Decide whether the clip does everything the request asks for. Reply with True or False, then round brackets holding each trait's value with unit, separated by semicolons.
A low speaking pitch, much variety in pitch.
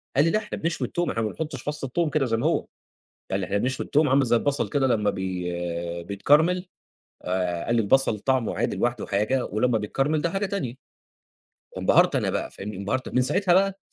True (130 Hz; 6.8 semitones)